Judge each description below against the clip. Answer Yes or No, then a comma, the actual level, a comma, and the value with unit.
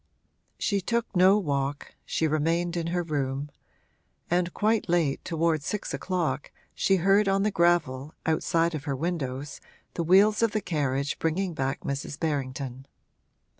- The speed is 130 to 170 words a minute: Yes, average, 145 wpm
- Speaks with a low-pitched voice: No, medium, 165 Hz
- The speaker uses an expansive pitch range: No, average, 4.7 semitones